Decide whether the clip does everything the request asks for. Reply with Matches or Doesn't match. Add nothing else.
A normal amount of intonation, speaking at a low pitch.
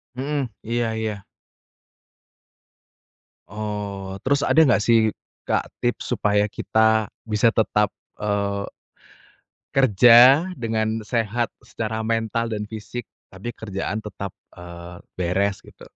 Doesn't match